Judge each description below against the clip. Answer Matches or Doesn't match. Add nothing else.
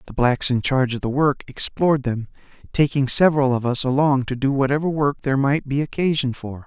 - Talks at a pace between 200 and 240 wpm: Matches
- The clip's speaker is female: Doesn't match